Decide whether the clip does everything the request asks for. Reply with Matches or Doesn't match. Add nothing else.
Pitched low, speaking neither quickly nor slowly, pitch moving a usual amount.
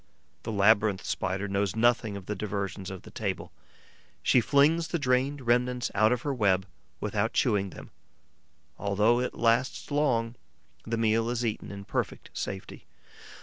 Matches